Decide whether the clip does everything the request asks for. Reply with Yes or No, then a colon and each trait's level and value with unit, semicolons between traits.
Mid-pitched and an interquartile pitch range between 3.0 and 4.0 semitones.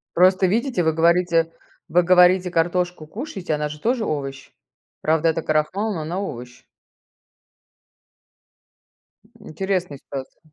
Yes: medium, 170 Hz; average, 3.3 semitones